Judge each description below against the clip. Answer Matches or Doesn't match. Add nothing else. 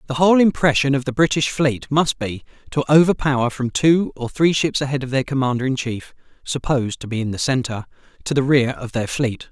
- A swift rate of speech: Matches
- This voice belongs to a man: Matches